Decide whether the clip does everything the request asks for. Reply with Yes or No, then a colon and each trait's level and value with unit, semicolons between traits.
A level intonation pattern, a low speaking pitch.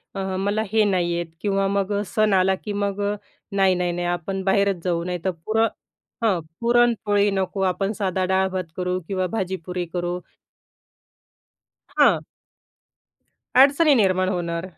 No: narrow, 2.0 semitones; high, 190 Hz